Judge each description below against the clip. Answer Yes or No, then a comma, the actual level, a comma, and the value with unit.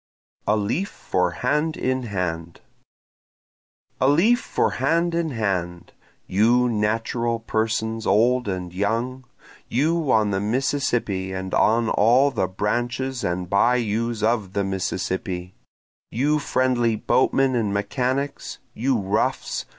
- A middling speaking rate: No, slow, 120 wpm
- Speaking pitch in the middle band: No, low, 115 Hz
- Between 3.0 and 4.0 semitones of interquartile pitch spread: No, average, 4.5 semitones